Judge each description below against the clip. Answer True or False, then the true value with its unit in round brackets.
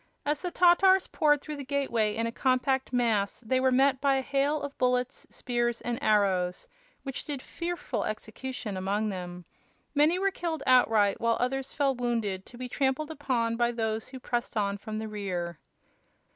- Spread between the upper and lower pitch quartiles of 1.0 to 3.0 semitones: False (4.3 semitones)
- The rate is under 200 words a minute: True (175 wpm)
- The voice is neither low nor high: False (250 Hz)